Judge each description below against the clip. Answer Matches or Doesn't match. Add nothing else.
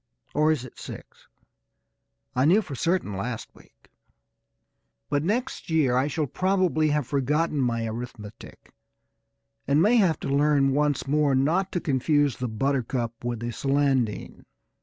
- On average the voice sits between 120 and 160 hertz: Matches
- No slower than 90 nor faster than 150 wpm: Matches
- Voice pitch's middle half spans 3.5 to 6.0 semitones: Matches